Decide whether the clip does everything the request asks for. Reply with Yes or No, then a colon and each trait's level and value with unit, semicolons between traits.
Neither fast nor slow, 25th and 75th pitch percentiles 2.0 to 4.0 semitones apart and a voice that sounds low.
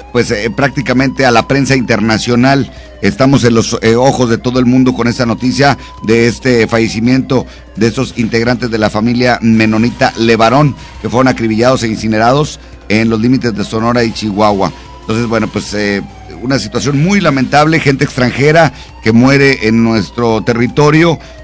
Yes: average, 160 wpm; average, 2.8 semitones; low, 120 Hz